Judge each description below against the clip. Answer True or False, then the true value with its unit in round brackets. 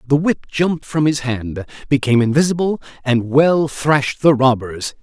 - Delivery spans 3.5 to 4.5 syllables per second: False (4.9 syllables/s)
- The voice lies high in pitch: False (140 Hz)